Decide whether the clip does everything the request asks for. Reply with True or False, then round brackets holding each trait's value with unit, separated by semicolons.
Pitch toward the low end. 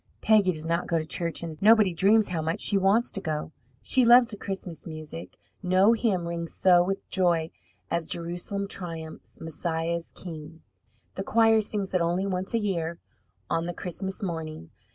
False (175 Hz)